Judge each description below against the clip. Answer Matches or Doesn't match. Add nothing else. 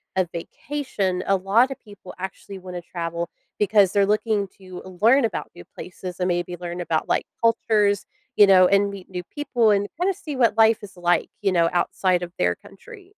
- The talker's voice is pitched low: Doesn't match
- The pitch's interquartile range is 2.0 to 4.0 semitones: Matches